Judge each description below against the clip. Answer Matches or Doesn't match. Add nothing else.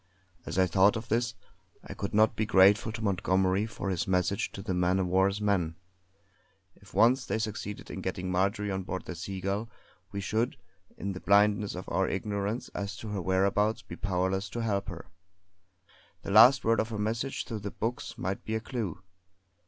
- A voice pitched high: Doesn't match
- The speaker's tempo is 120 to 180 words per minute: Doesn't match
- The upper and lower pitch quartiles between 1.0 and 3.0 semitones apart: Matches